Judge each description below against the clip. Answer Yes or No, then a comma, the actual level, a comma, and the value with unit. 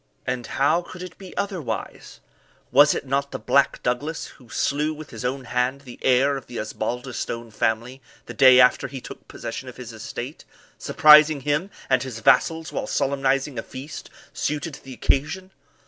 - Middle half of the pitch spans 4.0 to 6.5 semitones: No, average, 3.3 semitones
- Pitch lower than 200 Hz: Yes, low, 135 Hz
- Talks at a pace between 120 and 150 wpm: No, average, 175 wpm